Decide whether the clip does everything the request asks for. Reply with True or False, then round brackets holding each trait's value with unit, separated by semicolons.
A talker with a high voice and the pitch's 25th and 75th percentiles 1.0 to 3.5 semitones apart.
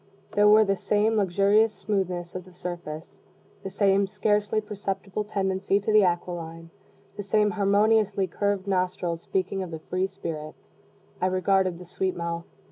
True (195 Hz; 2.4 semitones)